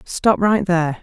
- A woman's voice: Yes, female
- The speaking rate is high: No, average, 175 wpm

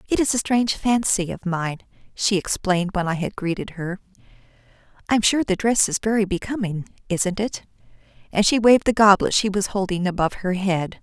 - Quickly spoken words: No, average, 180 wpm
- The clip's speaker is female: Yes, female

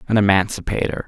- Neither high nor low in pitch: No, low, 100 Hz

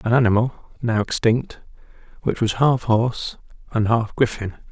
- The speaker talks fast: No, average, 140 wpm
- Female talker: No, male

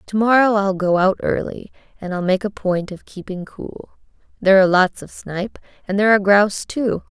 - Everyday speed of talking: Yes, average, 195 wpm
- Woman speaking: Yes, female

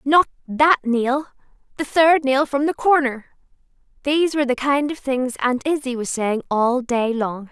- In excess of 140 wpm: Yes, average, 170 wpm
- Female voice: Yes, female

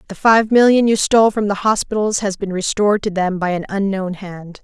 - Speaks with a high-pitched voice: Yes, high, 200 Hz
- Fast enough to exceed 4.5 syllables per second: Yes, 5.5 syllables/s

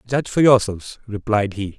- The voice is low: Yes, low, 110 Hz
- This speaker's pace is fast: No, average, 170 wpm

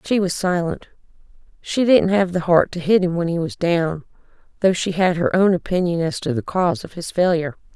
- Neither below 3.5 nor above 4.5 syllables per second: No, 5.5 syllables/s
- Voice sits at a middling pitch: Yes, medium, 175 Hz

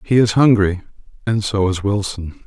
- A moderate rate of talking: Yes, average, 170 wpm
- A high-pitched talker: No, low, 100 Hz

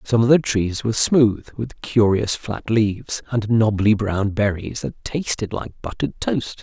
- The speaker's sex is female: No, male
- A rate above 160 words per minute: Yes, average, 170 wpm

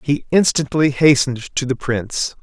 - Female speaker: No, male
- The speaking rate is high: No, average, 150 wpm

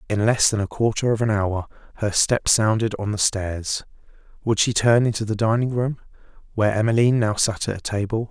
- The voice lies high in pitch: No, low, 110 Hz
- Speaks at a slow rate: No, average, 190 wpm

